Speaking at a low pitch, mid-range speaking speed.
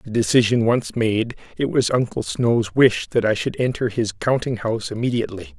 Yes: low, 115 Hz; average, 185 wpm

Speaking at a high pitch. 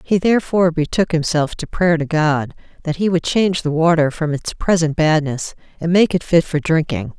No: medium, 160 Hz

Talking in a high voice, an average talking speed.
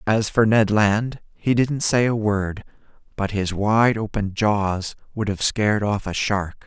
No: low, 105 Hz; average, 180 wpm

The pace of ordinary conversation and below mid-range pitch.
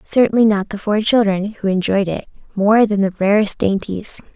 No: average, 180 wpm; high, 205 Hz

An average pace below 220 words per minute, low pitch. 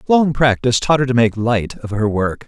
No: fast, 240 wpm; low, 120 Hz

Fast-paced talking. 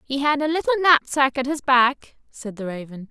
Yes: fast, 210 wpm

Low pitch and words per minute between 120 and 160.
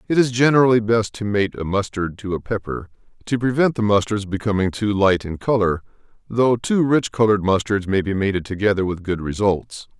No: low, 105 Hz; average, 190 wpm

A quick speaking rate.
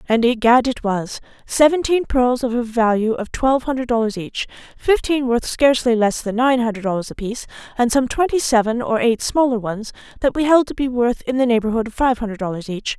Yes: fast, 210 wpm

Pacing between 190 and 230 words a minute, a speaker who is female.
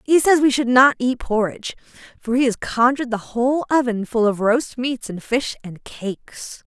Yes: average, 195 wpm; female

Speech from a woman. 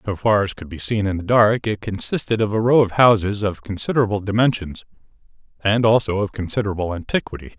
No: male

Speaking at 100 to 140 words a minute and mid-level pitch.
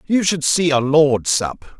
No: average, 200 wpm; medium, 150 Hz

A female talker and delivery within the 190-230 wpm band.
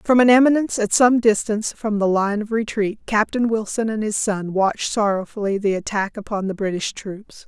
Yes: female; average, 195 wpm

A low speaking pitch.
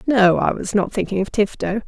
No: high, 205 Hz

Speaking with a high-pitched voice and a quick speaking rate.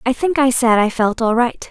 Yes: high, 245 Hz; fast, 280 wpm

